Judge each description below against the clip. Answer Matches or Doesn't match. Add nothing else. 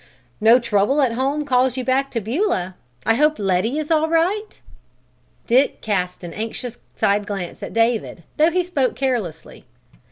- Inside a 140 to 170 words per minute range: Matches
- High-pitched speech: Matches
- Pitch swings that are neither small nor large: Doesn't match